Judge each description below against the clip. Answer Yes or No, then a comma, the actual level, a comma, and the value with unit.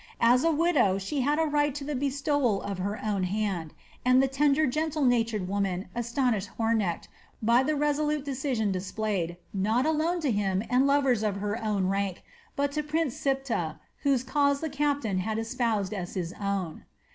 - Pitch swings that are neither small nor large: No, wide, 6.2 semitones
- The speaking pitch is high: Yes, high, 240 Hz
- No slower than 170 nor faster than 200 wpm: Yes, average, 175 wpm